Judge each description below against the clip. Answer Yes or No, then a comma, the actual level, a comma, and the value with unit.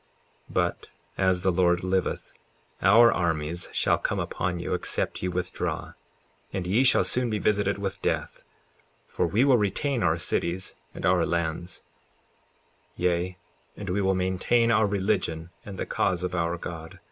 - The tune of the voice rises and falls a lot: No, average, 2.8 semitones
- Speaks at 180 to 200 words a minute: No, average, 160 wpm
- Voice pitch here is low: Yes, very low, 90 Hz